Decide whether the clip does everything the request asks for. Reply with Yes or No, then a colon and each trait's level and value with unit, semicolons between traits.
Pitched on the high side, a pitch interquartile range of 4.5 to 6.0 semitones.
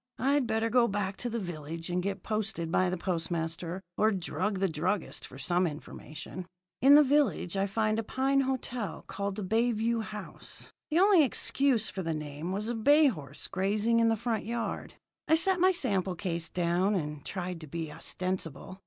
Yes: high, 200 Hz; average, 5.1 semitones